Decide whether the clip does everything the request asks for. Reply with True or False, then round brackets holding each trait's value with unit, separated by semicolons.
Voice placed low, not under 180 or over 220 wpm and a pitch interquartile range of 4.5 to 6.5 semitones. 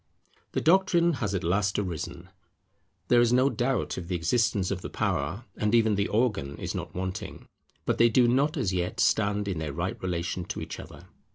True (105 Hz; 195 wpm; 4.9 semitones)